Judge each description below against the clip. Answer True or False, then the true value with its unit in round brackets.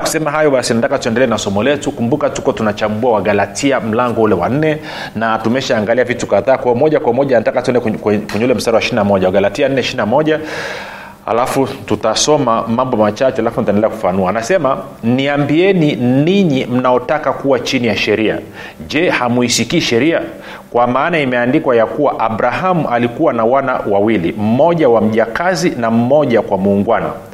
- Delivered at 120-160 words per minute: True (135 wpm)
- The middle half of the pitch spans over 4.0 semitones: True (4.5 semitones)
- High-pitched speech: False (125 Hz)